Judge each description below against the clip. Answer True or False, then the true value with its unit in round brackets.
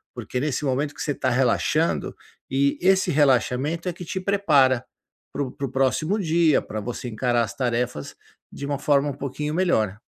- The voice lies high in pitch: False (140 Hz)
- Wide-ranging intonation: False (3.7 semitones)